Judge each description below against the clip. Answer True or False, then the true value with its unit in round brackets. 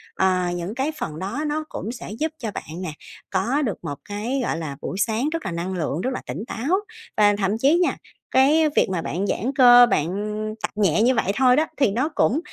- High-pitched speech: True (220 Hz)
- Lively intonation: True (6.2 semitones)